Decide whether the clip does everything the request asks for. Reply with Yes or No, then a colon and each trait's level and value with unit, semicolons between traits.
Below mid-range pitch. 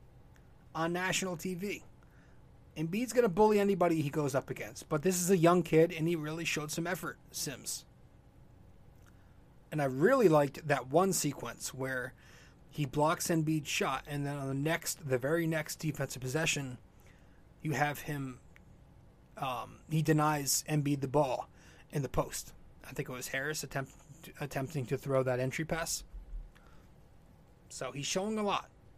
No: medium, 145 Hz